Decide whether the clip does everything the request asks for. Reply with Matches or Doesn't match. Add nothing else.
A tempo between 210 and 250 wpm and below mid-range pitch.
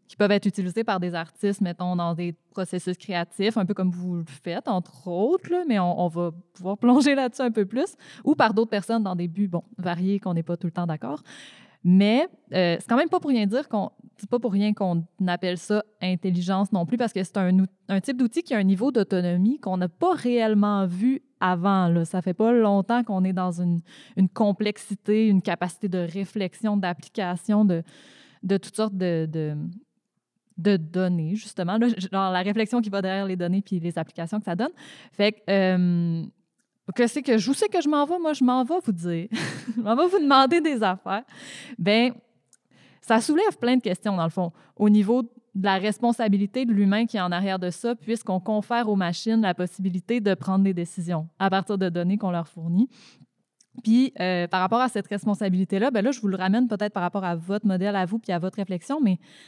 Doesn't match